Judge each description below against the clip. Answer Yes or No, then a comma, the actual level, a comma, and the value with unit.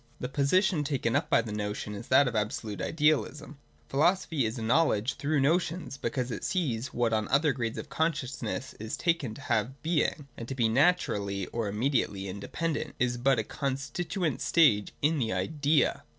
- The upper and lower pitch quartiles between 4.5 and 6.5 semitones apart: Yes, average, 5.3 semitones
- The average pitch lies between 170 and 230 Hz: No, low, 135 Hz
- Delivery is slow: No, average, 180 wpm